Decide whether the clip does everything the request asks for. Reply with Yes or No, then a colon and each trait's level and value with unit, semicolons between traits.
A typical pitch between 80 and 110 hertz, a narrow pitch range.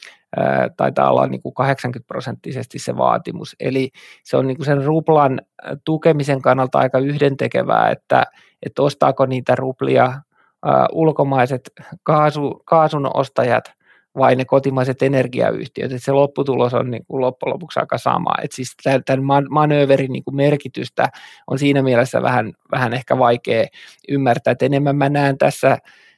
No: low, 135 Hz; narrow, 1.9 semitones